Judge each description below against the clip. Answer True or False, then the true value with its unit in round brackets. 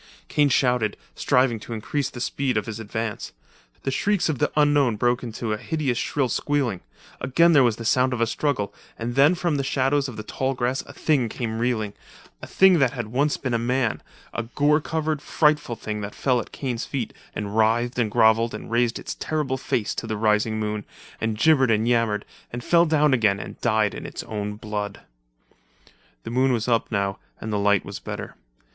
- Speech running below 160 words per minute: False (200 wpm)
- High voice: False (120 Hz)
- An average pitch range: True (4.0 semitones)